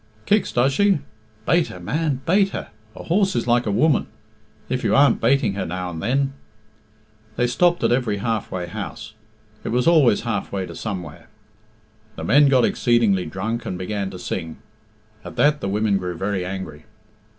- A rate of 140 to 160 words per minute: No, average, 180 wpm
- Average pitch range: No, wide, 6.2 semitones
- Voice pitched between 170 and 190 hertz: No, low, 110 Hz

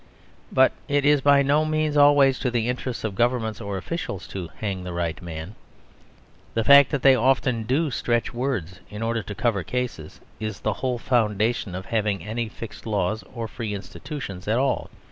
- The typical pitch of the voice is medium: No, low, 115 Hz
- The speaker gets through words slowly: No, average, 185 wpm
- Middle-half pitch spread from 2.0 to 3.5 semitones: No, average, 4.6 semitones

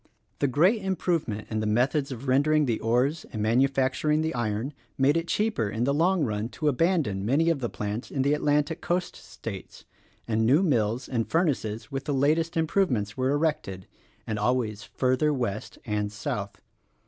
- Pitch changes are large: Yes, wide, 5.7 semitones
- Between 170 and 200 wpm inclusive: Yes, average, 175 wpm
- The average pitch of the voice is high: No, low, 135 Hz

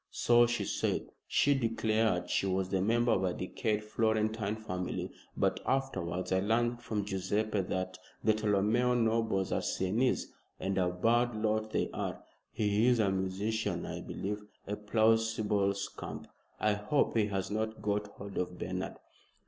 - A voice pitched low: Yes, low, 105 Hz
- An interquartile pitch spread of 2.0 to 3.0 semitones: Yes, average, 2.7 semitones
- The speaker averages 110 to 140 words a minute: No, average, 155 wpm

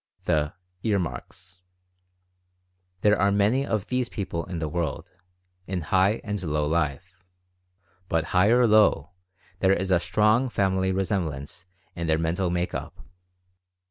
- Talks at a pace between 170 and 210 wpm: No, average, 140 wpm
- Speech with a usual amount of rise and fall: Yes, average, 3.6 semitones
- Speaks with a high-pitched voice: No, very low, 95 Hz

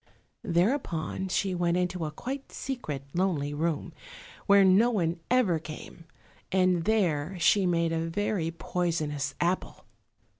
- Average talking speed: No, slow, 125 wpm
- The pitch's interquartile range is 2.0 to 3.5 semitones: Yes, average, 3.0 semitones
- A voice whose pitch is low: No, medium, 175 Hz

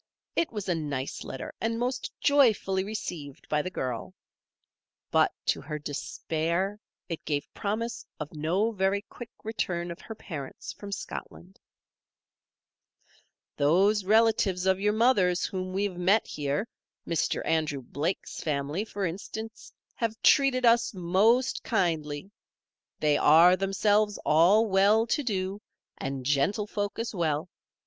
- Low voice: No, high, 190 Hz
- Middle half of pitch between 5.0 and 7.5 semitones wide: Yes, average, 5.3 semitones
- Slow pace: Yes, slow, 130 wpm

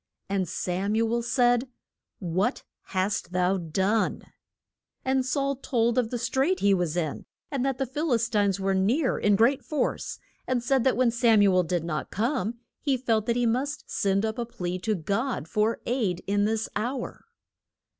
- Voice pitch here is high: Yes, high, 225 Hz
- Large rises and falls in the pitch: No, average, 4.5 semitones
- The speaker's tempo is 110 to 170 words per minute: No, average, 185 wpm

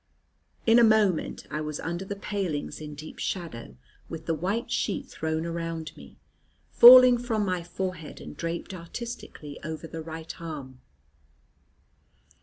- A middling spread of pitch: Yes, average, 4.3 semitones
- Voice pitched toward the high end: No, medium, 170 Hz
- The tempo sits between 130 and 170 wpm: Yes, average, 140 wpm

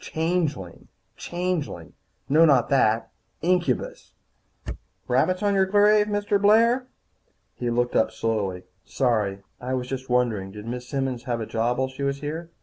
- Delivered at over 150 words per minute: Yes, average, 160 wpm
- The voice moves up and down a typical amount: No, wide, 7.2 semitones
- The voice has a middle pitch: No, low, 130 Hz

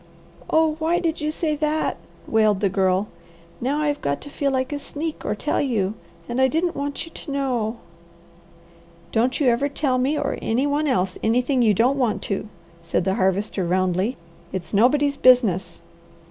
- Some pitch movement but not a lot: No, wide, 6.1 semitones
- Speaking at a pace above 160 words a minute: Yes, average, 175 wpm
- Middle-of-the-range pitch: No, very high, 255 Hz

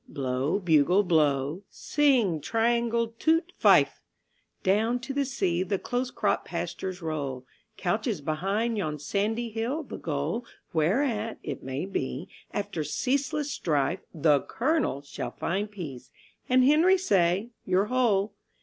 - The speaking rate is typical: No, slow, 130 wpm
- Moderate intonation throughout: No, wide, 7.4 semitones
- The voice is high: Yes, high, 195 Hz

